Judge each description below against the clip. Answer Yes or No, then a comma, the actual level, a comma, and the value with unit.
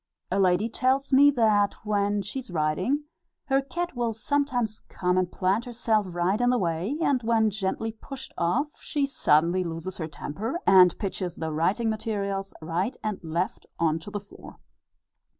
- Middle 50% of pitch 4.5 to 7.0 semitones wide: Yes, average, 5.2 semitones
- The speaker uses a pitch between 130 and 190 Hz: No, high, 205 Hz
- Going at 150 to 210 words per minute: Yes, average, 170 wpm